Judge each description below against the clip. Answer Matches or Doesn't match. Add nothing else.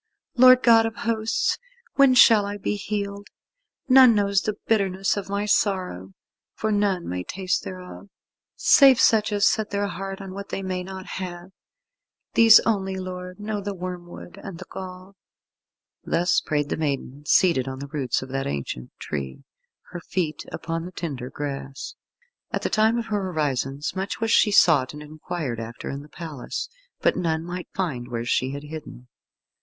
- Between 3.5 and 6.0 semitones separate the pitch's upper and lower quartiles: Matches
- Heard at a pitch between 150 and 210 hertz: Matches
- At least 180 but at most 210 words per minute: Doesn't match